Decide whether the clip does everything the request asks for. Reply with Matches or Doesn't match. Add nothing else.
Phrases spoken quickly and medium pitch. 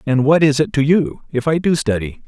Matches